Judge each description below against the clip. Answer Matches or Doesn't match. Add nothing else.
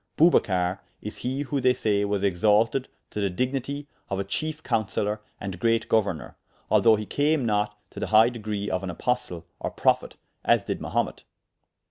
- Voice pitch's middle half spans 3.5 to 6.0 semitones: Matches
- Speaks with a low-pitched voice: Matches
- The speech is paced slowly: Doesn't match